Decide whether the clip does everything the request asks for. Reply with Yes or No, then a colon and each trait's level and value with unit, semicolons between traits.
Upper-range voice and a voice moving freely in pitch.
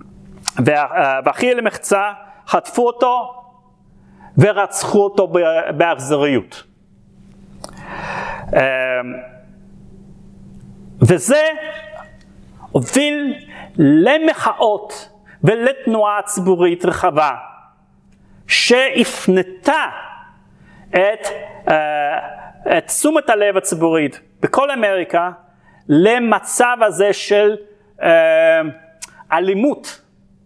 Yes: high, 205 Hz; wide, 6.2 semitones